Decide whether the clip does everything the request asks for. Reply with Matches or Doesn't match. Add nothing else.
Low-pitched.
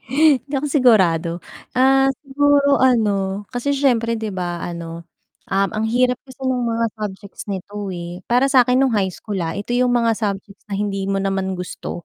Doesn't match